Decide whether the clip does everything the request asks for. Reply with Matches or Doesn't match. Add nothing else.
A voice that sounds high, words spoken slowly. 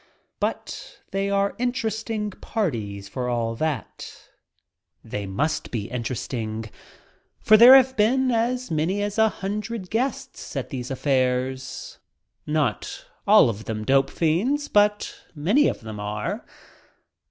Doesn't match